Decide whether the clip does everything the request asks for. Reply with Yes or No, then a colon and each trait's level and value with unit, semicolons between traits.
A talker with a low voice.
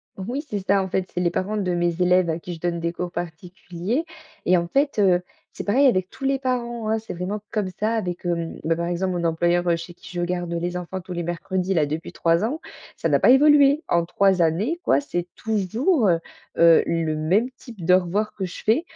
No: medium, 180 Hz